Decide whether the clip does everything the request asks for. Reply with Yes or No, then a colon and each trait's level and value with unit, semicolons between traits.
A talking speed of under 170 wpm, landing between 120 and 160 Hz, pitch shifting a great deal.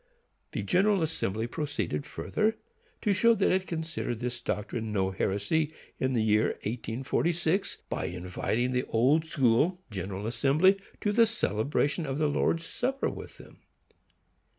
Yes: average, 140 wpm; medium, 140 Hz; wide, 7.7 semitones